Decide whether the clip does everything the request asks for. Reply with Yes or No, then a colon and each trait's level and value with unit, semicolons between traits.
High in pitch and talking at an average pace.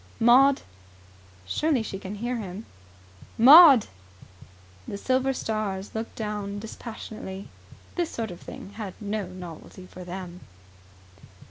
No: high, 215 Hz; slow, 115 wpm